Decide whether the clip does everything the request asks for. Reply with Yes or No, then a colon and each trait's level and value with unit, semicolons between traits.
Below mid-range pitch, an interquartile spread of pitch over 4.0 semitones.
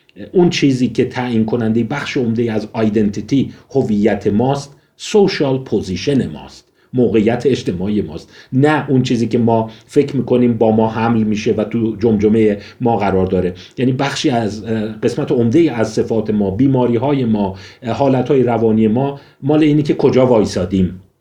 No: low, 115 Hz; average, 3.5 semitones